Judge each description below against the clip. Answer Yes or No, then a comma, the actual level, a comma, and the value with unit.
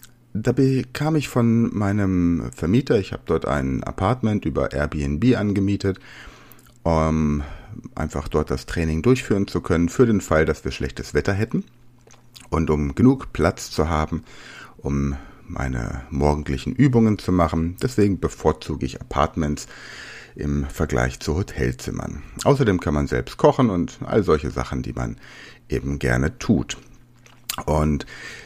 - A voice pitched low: Yes, very low, 85 Hz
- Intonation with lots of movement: Yes, wide, 7.9 semitones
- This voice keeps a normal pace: Yes, average, 135 wpm